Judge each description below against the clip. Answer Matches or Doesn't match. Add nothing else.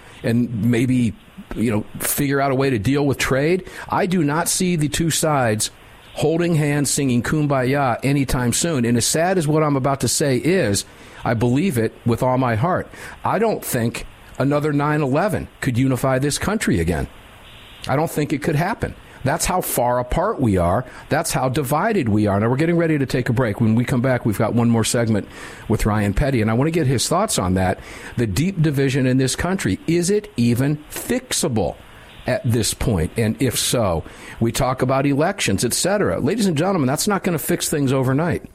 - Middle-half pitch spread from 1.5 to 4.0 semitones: Doesn't match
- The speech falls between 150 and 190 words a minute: Doesn't match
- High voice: Doesn't match